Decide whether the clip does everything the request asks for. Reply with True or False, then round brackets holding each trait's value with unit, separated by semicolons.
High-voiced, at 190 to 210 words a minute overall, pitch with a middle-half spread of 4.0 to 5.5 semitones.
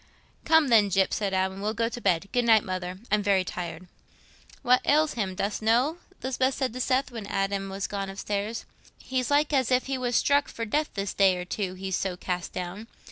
True (210 Hz; 205 wpm; 4.8 semitones)